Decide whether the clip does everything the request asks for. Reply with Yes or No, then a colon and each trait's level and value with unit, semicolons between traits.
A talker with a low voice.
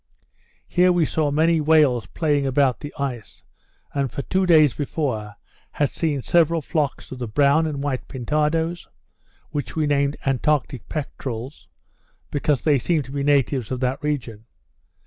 No: medium, 145 Hz